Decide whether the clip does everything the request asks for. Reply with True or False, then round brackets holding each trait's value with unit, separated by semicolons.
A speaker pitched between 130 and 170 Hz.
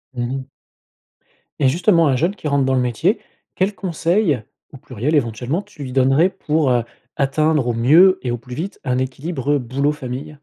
True (140 Hz)